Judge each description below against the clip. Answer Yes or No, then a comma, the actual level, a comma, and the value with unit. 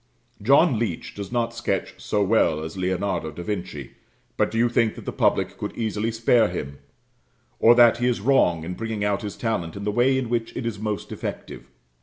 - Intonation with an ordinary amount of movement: Yes, average, 4.1 semitones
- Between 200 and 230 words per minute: Yes, fast, 205 wpm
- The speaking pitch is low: Yes, low, 105 Hz